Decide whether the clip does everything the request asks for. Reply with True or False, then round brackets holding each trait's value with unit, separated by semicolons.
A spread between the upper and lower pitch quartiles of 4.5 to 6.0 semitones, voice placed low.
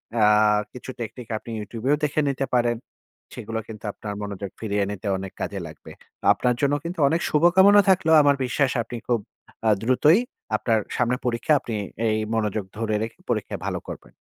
True (4.8 semitones; 120 Hz)